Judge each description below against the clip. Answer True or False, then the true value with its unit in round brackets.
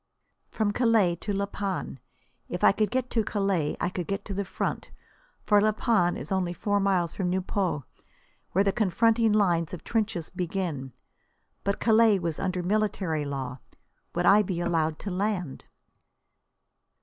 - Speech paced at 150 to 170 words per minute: True (160 wpm)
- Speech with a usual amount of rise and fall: True (3.2 semitones)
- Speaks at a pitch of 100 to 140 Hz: False (190 Hz)